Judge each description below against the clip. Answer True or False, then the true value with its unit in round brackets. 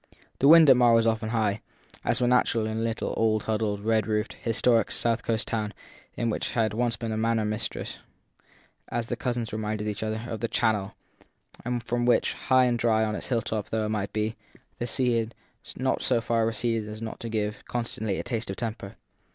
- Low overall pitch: True (115 Hz)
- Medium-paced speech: False (210 wpm)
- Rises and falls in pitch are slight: True (1.6 semitones)